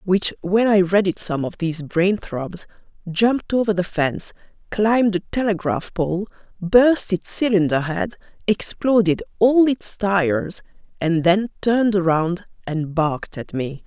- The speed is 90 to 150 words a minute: Yes, average, 145 wpm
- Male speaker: No, female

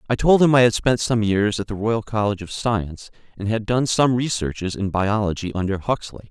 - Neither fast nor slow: No, fast, 220 wpm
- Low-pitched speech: Yes, low, 110 Hz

